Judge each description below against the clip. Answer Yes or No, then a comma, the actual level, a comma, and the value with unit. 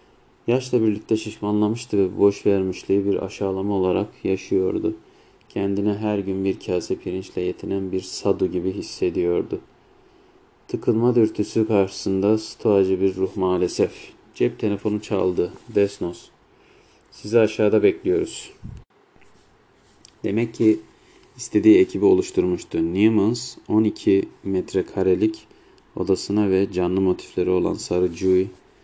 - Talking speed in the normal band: Yes, average, 105 wpm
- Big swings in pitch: No, average, 4.3 semitones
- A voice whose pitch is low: Yes, low, 105 Hz